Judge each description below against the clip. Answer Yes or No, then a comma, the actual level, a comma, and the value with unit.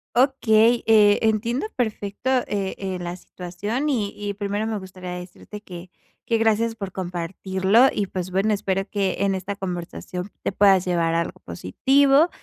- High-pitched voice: Yes, high, 200 Hz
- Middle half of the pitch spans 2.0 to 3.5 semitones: Yes, average, 3.2 semitones